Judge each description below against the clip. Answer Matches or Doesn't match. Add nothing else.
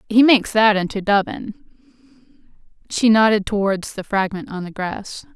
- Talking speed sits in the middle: Matches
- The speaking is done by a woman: Matches